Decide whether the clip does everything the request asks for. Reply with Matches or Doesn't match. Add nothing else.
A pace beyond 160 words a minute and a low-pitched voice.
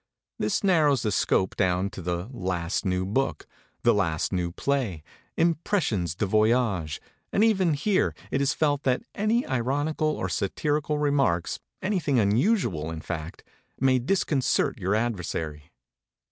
Doesn't match